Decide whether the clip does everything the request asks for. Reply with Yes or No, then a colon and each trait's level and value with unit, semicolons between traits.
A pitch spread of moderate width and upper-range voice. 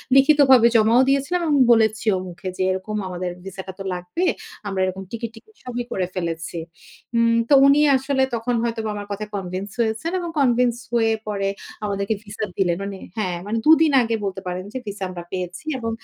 Yes: average, 4.5 semitones; high, 215 Hz